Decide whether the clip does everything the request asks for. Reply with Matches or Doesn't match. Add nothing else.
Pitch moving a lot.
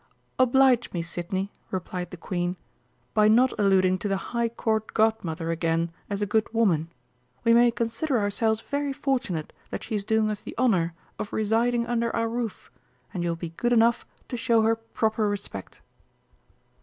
Doesn't match